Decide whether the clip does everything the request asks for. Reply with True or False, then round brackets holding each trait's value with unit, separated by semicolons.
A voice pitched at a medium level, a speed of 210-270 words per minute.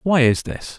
True (145 Hz; 230 wpm)